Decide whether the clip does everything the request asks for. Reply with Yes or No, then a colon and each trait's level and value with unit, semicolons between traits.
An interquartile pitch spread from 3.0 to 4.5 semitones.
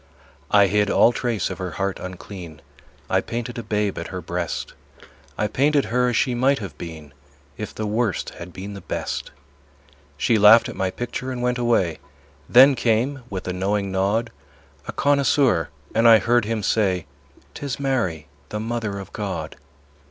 Yes: average, 4.1 semitones